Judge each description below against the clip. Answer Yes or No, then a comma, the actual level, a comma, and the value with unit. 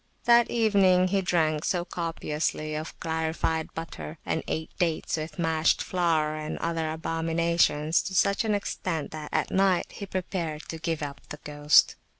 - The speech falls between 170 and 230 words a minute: No, average, 155 wpm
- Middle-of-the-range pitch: Yes, medium, 165 Hz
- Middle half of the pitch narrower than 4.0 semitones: Yes, narrow, 2.6 semitones